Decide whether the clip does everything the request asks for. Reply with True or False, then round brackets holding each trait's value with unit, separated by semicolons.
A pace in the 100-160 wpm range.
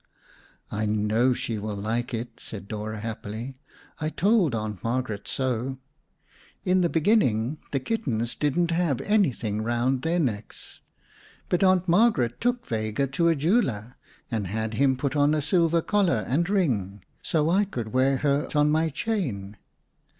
True (150 wpm)